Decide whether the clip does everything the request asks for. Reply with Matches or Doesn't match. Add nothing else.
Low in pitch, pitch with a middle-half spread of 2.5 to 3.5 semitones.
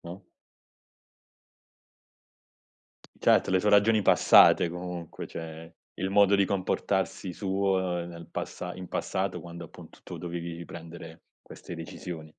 Doesn't match